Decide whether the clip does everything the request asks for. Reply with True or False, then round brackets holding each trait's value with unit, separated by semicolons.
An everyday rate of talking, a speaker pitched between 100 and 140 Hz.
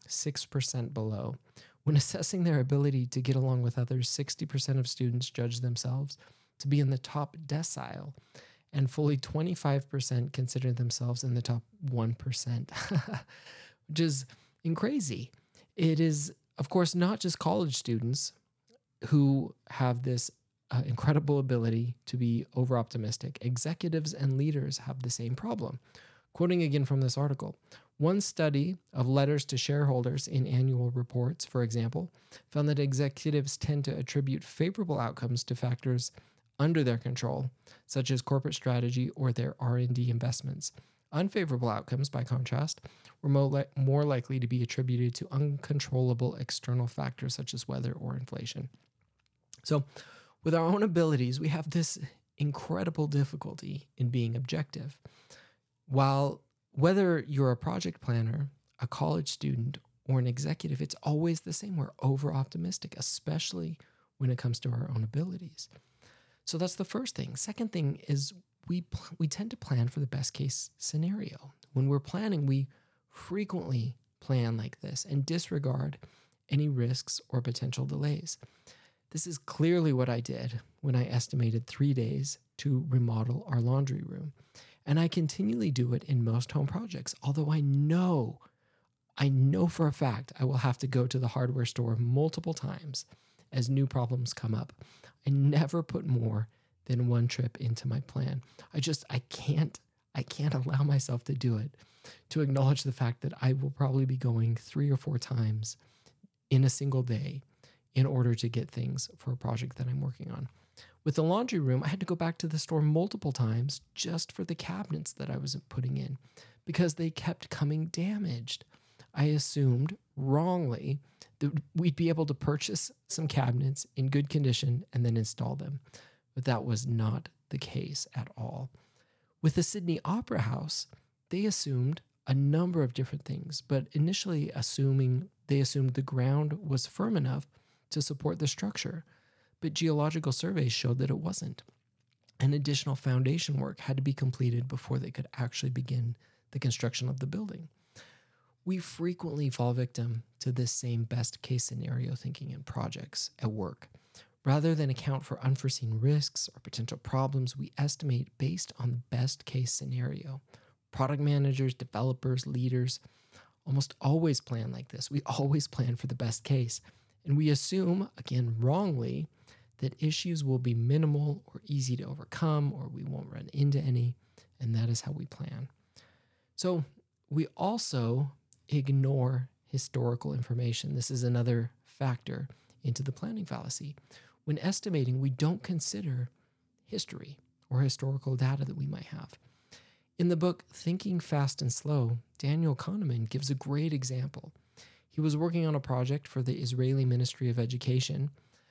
True (155 wpm; 135 Hz)